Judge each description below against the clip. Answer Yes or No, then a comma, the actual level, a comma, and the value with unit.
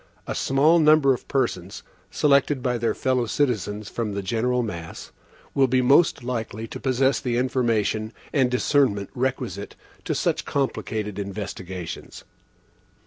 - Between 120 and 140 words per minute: Yes, slow, 135 wpm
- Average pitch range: Yes, average, 4.1 semitones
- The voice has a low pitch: Yes, low, 125 Hz